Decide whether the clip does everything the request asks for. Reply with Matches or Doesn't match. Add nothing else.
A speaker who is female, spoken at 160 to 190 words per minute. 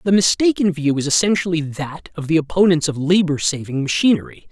Doesn't match